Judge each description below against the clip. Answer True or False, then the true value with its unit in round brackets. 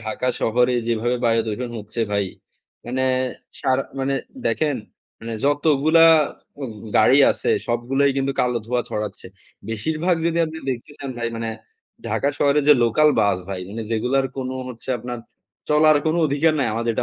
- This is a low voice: True (125 Hz)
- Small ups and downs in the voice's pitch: False (3.7 semitones)